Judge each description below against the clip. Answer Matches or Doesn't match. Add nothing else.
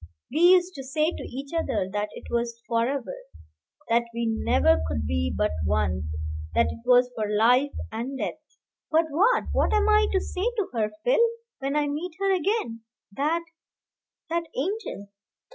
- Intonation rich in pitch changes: Matches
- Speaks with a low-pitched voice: Doesn't match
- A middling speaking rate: Matches